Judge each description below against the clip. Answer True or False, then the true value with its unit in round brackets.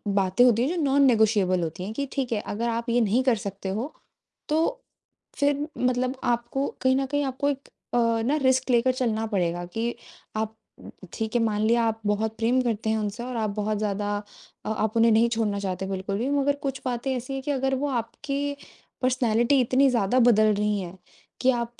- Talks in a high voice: True (235 Hz)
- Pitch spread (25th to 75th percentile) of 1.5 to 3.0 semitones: False (3.5 semitones)